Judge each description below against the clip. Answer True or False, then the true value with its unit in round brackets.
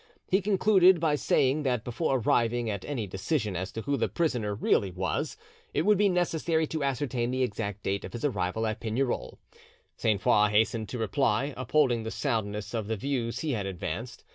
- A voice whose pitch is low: True (120 Hz)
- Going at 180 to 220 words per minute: True (190 wpm)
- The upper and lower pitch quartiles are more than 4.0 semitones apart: True (5.5 semitones)